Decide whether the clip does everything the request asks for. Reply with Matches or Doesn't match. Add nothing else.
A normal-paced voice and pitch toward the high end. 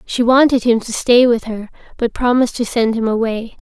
Doesn't match